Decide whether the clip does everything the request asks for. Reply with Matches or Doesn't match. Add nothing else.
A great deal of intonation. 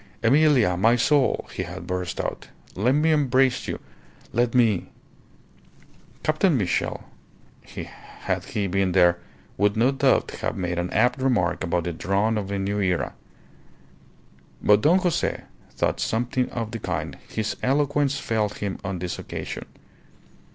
Matches